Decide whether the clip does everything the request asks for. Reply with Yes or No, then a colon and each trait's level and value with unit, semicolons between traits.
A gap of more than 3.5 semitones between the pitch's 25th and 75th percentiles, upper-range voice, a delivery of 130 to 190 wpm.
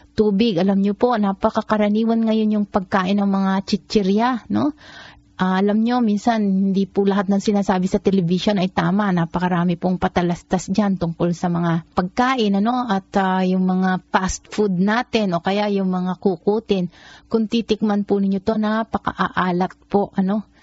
No: narrow, 2.5 semitones; high, 200 Hz; fast, 155 wpm